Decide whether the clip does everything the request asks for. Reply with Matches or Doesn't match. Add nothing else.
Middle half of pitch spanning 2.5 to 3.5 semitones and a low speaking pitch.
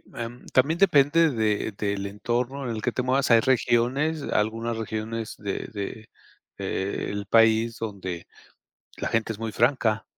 Matches